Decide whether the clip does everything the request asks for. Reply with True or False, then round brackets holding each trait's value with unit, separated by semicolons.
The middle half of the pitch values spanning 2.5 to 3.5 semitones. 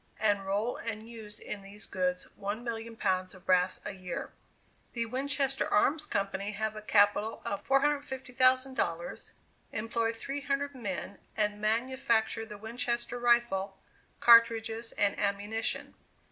True (3.1 semitones)